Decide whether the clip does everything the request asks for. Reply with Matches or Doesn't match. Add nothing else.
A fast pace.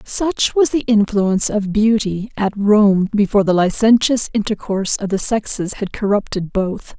Doesn't match